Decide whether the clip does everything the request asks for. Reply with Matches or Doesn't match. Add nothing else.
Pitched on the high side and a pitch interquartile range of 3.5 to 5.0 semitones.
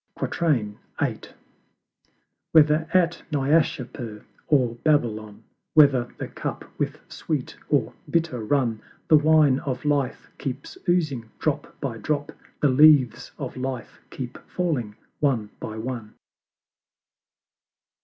Doesn't match